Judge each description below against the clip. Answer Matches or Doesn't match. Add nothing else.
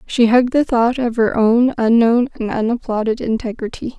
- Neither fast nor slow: Matches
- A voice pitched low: Doesn't match